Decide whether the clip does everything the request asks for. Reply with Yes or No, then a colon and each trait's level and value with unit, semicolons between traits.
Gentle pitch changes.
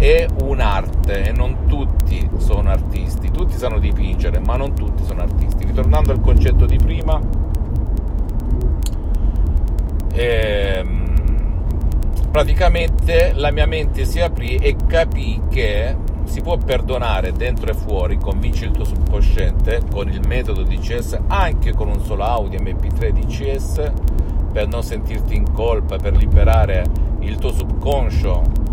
Yes: narrow, 2.2 semitones